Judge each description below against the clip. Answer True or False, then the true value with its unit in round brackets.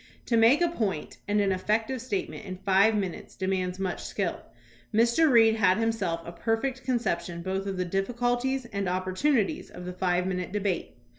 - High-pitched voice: True (200 Hz)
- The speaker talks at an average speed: True (175 wpm)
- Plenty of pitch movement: False (4.1 semitones)